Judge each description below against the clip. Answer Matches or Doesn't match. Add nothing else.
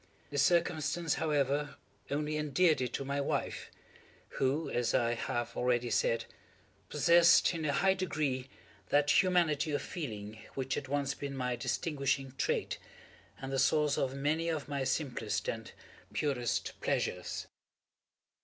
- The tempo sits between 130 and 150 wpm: Matches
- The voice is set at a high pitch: Doesn't match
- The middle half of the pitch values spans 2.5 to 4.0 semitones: Matches